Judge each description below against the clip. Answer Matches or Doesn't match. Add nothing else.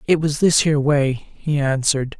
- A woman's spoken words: Doesn't match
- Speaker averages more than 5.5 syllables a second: Doesn't match